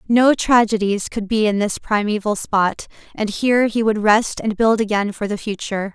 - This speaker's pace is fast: No, average, 190 wpm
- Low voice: No, high, 215 Hz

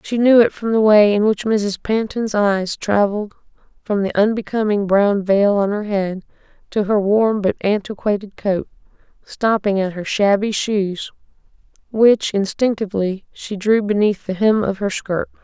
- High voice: Yes, high, 205 Hz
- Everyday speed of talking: Yes, average, 160 wpm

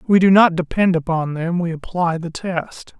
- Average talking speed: Yes, average, 180 wpm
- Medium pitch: Yes, medium, 170 Hz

